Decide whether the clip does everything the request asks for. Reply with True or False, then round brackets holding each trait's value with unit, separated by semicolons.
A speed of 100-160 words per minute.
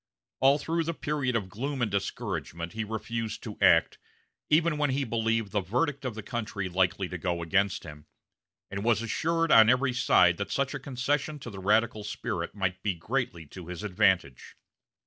False (185 wpm)